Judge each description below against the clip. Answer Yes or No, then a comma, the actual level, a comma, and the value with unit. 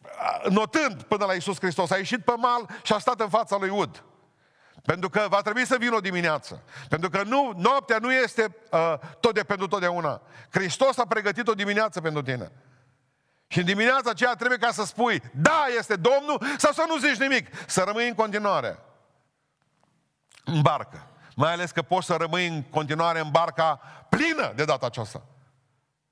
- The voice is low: No, high, 195 Hz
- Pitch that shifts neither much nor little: No, wide, 6.8 semitones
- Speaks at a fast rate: Yes, fast, 180 wpm